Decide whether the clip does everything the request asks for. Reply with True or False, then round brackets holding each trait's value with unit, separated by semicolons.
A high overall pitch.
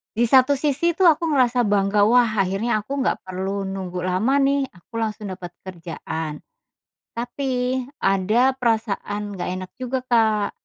True (220 Hz)